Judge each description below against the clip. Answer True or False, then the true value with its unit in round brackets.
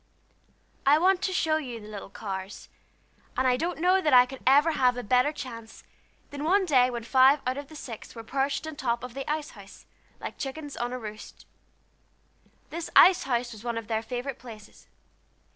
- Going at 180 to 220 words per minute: True (195 wpm)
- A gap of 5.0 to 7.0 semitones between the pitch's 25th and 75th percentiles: False (4.3 semitones)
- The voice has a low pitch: False (255 Hz)